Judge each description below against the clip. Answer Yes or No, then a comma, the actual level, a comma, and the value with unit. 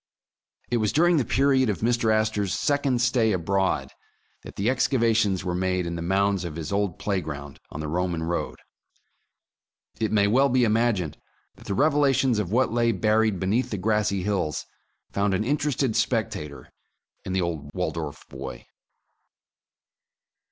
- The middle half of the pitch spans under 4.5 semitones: No, average, 4.8 semitones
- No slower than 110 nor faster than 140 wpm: No, average, 155 wpm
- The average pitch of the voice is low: Yes, low, 105 Hz